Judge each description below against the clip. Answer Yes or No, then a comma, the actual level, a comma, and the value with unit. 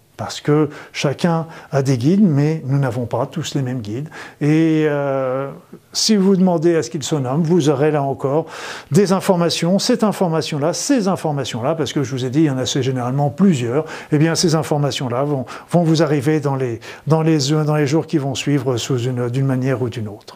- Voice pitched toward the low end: No, medium, 150 Hz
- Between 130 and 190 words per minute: No, average, 210 wpm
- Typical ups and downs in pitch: Yes, average, 3.2 semitones